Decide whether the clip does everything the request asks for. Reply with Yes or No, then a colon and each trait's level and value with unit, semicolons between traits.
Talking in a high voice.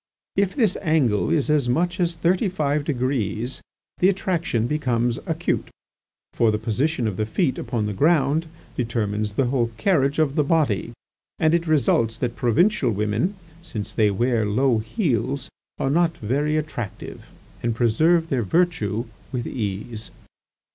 No: low, 130 Hz